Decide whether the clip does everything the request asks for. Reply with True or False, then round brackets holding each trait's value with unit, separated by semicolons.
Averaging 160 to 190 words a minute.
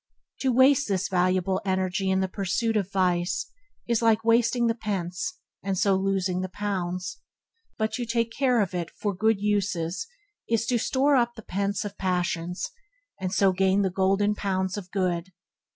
True (170 wpm)